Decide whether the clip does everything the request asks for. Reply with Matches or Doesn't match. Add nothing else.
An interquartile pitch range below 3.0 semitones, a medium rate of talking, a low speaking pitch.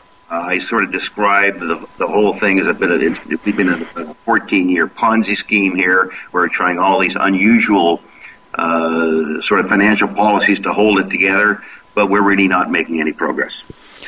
Matches